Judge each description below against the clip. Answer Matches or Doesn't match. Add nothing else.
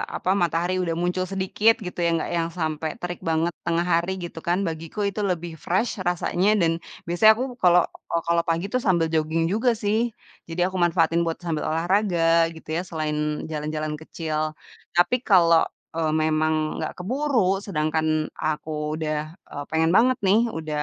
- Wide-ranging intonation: Doesn't match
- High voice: Doesn't match